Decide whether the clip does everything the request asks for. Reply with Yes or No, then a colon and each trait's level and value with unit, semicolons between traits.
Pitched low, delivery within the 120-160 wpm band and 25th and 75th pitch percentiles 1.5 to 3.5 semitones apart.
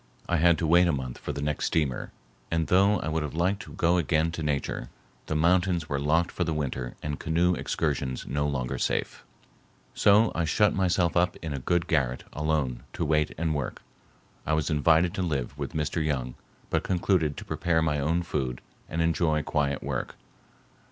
No: very low, 80 Hz; average, 190 wpm; average, 3.1 semitones